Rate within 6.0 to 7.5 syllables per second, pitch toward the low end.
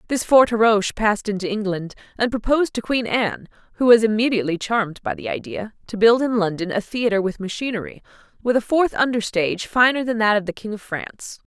No: 6.1 syllables/s; high, 220 Hz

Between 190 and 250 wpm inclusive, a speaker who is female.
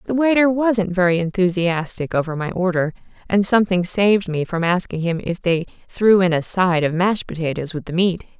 Yes: average, 195 wpm; female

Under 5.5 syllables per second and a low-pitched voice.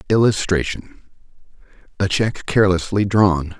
Yes: 4.8 syllables/s; low, 100 Hz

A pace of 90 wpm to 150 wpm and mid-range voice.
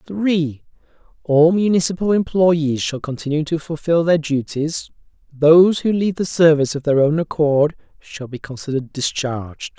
Yes: average, 140 wpm; medium, 155 Hz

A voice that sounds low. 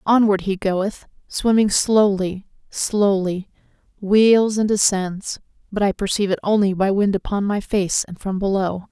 No: high, 200 Hz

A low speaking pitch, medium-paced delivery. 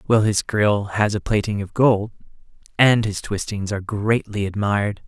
Yes: low, 105 Hz; average, 165 wpm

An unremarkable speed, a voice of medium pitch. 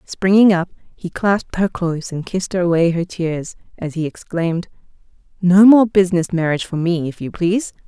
Yes: average, 175 wpm; medium, 180 Hz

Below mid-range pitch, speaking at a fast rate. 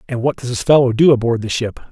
Yes: low, 125 Hz; fast, 285 wpm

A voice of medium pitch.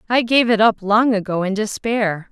No: high, 215 Hz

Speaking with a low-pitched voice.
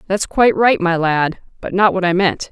No: medium, 185 Hz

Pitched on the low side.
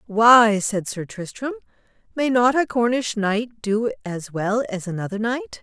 No: high, 225 Hz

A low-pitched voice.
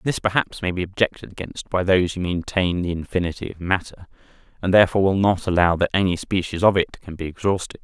Yes: very low, 90 Hz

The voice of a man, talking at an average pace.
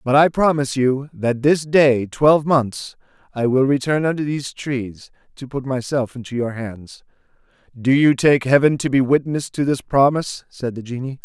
Yes: male; average, 180 wpm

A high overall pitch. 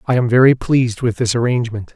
No: low, 120 Hz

